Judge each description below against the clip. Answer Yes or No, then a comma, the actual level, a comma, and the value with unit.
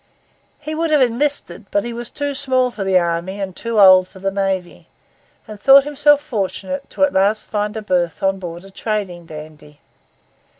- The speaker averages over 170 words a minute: Yes, average, 185 wpm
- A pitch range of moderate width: No, wide, 6.0 semitones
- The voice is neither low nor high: No, high, 205 Hz